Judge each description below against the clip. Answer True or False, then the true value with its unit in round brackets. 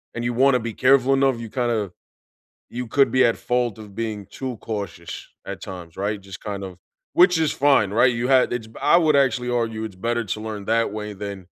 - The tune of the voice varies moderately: True (3.5 semitones)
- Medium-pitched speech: False (115 Hz)